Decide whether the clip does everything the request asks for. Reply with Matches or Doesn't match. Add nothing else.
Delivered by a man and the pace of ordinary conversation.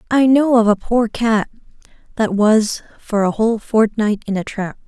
Doesn't match